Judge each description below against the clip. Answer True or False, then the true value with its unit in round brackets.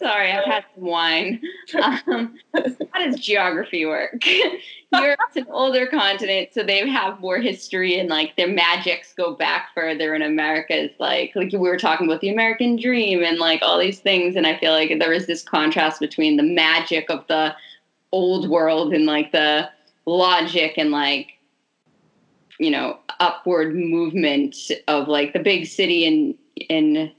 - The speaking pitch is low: False (185 Hz)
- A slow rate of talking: False (170 wpm)